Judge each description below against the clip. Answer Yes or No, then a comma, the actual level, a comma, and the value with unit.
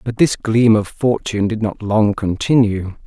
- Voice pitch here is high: No, low, 110 Hz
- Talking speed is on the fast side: No, average, 175 wpm